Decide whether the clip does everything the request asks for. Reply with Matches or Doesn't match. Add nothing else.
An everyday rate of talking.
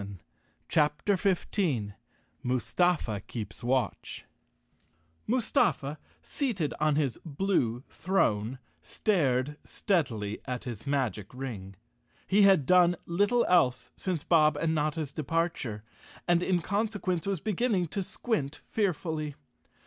Doesn't match